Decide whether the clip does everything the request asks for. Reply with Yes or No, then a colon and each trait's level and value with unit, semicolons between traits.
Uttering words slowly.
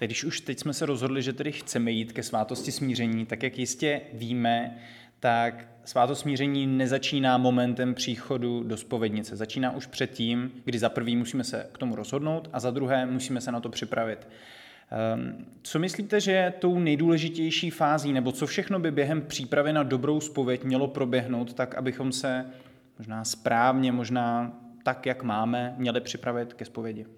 No: average, 165 wpm